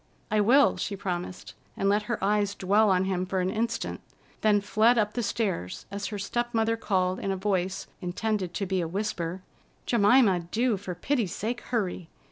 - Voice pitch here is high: Yes, high, 200 Hz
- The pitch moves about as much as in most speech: Yes, average, 3.1 semitones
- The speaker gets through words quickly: No, average, 185 wpm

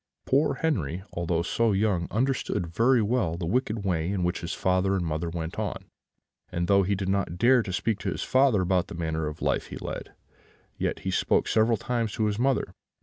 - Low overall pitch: Yes, very low, 95 Hz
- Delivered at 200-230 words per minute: Yes, fast, 205 wpm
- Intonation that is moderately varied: Yes, average, 4.8 semitones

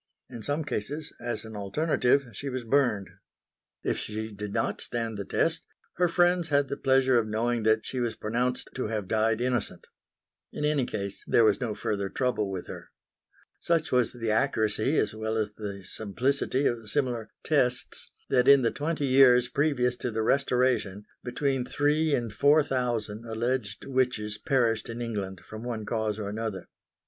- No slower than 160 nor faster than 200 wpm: Yes, average, 170 wpm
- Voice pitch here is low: Yes, low, 120 Hz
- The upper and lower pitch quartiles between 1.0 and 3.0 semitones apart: No, average, 3.8 semitones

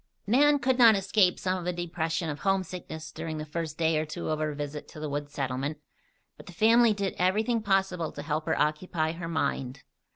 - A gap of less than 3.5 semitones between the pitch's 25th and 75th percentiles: No, average, 4.1 semitones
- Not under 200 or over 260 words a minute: Yes, fast, 205 wpm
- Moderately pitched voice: Yes, medium, 165 Hz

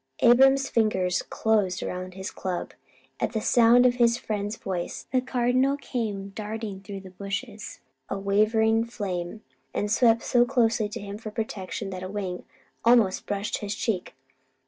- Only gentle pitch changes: No, average, 3.2 semitones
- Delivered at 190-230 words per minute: No, average, 155 wpm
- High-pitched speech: Yes, high, 215 Hz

